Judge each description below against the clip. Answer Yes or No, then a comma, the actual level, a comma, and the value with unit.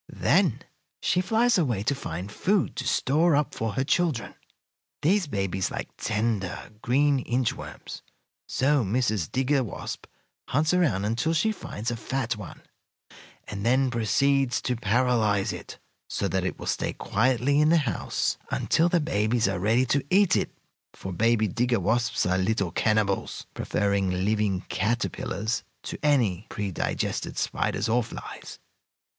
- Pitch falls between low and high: No, low, 120 Hz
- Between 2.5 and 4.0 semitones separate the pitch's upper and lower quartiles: No, average, 5.3 semitones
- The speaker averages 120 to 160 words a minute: Yes, average, 150 wpm